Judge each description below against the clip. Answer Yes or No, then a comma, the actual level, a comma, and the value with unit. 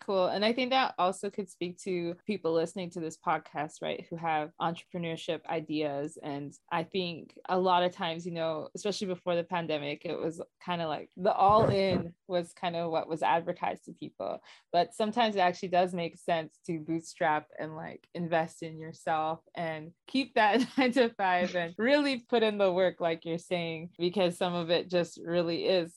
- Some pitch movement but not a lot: No, narrow, 2.2 semitones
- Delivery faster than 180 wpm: Yes, average, 195 wpm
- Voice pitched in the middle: Yes, medium, 175 Hz